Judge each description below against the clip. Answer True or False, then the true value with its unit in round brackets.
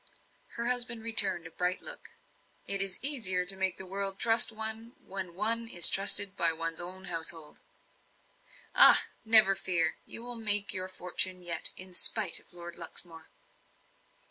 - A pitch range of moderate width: True (3.8 semitones)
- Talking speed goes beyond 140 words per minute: True (155 wpm)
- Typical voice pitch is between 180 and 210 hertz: True (190 Hz)